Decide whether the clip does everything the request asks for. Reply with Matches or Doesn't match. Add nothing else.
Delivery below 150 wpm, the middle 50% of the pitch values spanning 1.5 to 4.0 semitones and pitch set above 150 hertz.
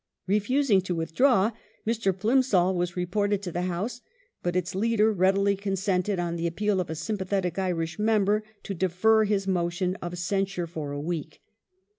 Doesn't match